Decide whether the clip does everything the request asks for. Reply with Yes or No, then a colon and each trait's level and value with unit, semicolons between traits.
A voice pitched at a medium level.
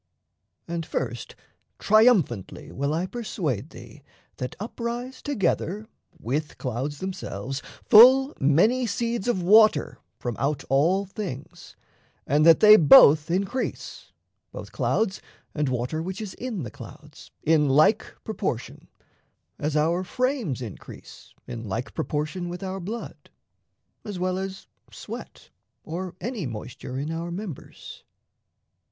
Yes: medium, 175 Hz